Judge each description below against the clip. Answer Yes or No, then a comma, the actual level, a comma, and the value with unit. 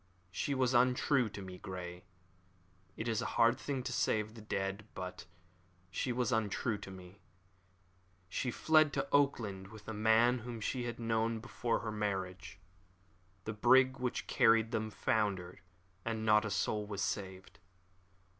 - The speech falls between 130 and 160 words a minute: Yes, average, 155 wpm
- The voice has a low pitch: Yes, low, 110 Hz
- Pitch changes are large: No, average, 3.5 semitones